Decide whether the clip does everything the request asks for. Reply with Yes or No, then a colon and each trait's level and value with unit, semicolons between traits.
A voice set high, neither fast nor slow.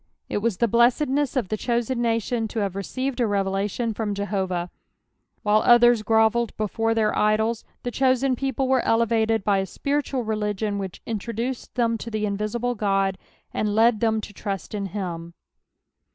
Yes: high, 220 Hz; average, 165 wpm